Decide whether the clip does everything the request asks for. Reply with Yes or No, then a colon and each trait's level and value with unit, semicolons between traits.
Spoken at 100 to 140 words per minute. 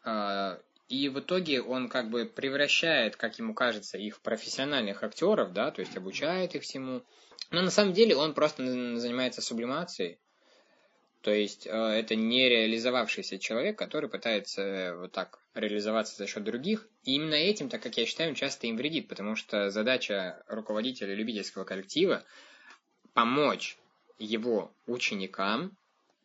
Yes: average, 135 wpm